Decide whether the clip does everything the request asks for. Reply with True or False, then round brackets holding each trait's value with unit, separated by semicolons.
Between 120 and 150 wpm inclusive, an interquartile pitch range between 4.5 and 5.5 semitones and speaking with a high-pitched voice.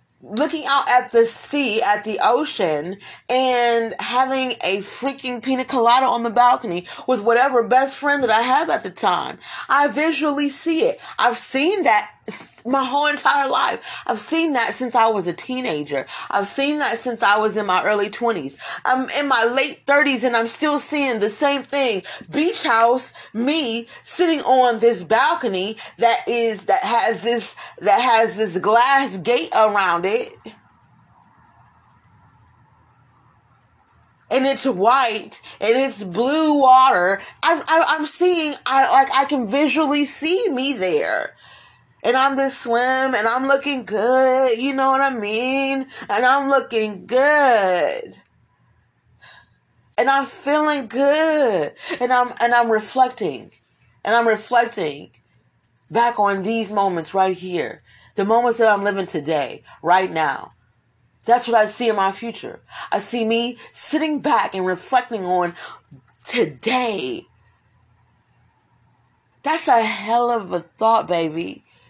True (145 wpm; 5.0 semitones; 240 Hz)